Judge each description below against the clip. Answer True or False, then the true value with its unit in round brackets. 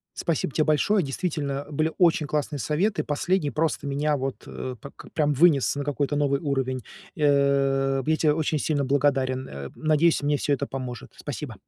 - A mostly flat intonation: True (2.2 semitones)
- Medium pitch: True (145 Hz)